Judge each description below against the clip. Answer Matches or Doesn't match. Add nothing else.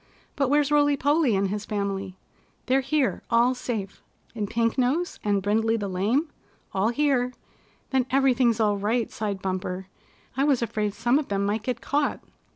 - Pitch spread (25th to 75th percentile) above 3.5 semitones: Matches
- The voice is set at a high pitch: Matches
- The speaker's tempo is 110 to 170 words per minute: Matches